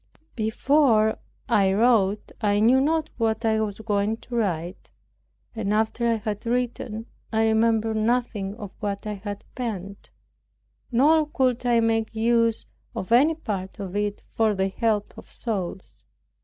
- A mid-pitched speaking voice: No, high, 220 Hz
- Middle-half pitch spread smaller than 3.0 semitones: Yes, narrow, 2.4 semitones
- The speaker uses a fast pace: No, average, 145 wpm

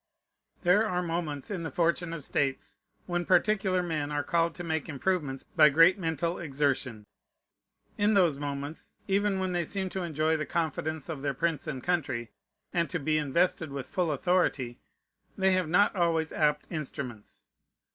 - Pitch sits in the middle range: Yes, medium, 165 Hz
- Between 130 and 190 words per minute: Yes, average, 165 wpm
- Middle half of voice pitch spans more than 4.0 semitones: No, average, 3.7 semitones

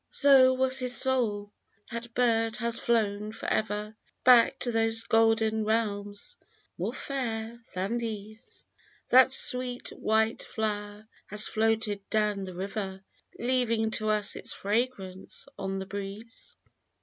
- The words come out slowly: Yes, slow, 125 wpm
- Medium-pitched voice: No, high, 220 Hz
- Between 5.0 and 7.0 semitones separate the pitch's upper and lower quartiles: No, narrow, 2.4 semitones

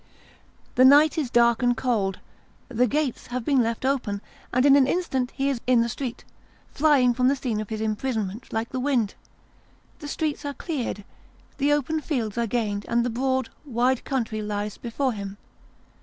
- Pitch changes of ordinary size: Yes, average, 3.5 semitones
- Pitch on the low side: No, very high, 250 Hz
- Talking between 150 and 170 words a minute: No, average, 180 wpm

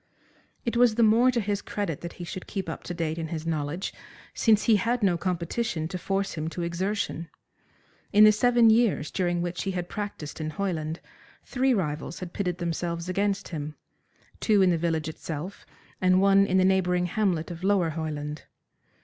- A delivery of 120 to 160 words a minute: No, average, 185 wpm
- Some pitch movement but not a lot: Yes, average, 3.6 semitones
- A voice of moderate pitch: Yes, medium, 180 Hz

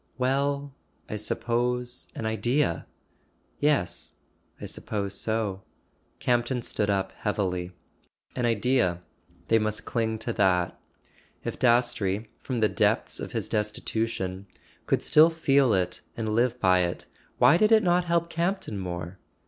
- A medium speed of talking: No, slow, 130 wpm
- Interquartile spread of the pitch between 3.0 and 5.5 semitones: Yes, average, 4.6 semitones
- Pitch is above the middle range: No, low, 115 Hz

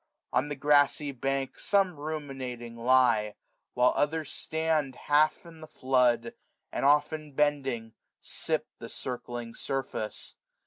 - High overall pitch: No, low, 135 Hz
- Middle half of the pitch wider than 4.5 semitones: No, average, 3.3 semitones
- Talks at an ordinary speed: No, slow, 120 wpm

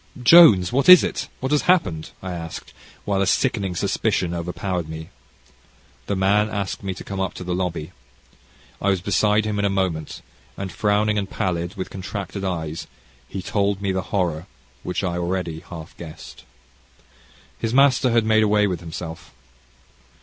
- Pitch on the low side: Yes, very low, 95 Hz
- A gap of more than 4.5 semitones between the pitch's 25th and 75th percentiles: No, average, 3.1 semitones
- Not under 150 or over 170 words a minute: Yes, average, 165 wpm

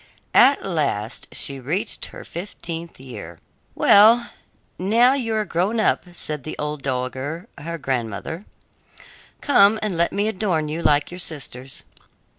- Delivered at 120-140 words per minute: Yes, slow, 135 wpm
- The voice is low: No, medium, 170 Hz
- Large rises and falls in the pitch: Yes, wide, 6.6 semitones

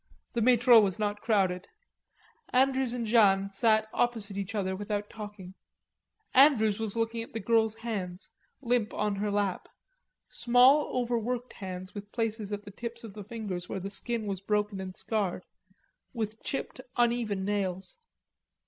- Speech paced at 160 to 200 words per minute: No, average, 150 wpm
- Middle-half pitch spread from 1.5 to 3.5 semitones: Yes, average, 2.9 semitones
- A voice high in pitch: Yes, high, 215 Hz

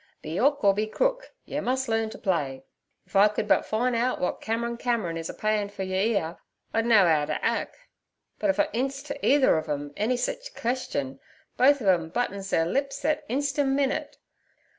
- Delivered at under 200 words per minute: No, fast, 205 wpm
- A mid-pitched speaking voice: No, high, 225 Hz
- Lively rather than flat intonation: Yes, wide, 6.2 semitones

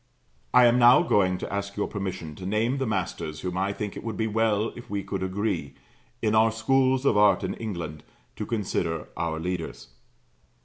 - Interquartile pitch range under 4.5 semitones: Yes, average, 3.6 semitones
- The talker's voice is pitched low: Yes, low, 100 Hz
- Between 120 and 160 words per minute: No, average, 190 wpm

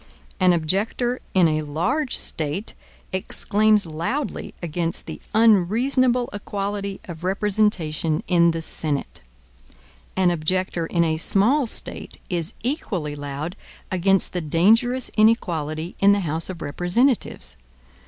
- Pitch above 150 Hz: Yes, medium, 185 Hz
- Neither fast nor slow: No, slow, 115 wpm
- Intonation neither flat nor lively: Yes, average, 4.8 semitones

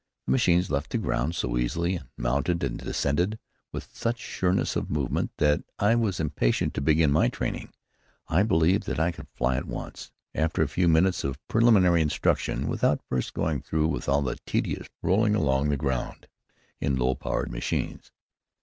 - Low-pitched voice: Yes, very low, 80 Hz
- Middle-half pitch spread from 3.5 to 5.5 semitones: Yes, average, 4.7 semitones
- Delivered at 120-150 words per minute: No, average, 175 wpm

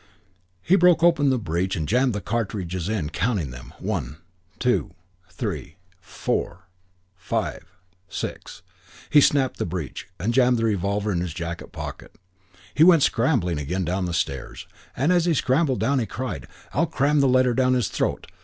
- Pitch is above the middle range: No, low, 110 Hz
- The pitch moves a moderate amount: No, wide, 7.2 semitones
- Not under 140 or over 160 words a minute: No, average, 170 wpm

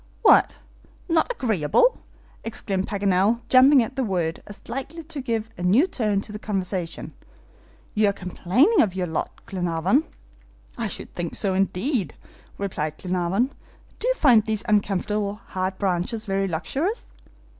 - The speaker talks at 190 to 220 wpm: No, average, 145 wpm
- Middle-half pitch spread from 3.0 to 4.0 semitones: No, average, 5.2 semitones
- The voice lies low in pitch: No, high, 205 Hz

